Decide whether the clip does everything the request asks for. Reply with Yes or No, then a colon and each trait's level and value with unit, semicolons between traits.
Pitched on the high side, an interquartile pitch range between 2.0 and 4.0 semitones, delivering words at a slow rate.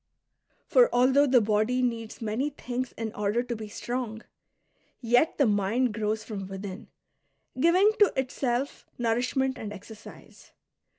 Yes: high, 240 Hz; average, 3.2 semitones; slow, 130 wpm